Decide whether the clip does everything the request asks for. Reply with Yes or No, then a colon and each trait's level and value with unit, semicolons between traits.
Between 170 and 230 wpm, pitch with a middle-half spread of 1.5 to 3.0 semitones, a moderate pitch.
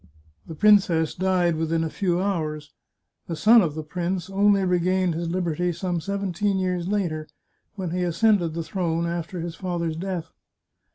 No: average, 160 wpm; narrow, 2.5 semitones; medium, 175 Hz